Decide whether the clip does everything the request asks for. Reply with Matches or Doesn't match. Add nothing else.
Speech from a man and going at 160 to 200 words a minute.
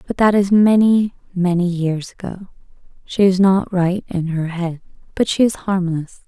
Doesn't match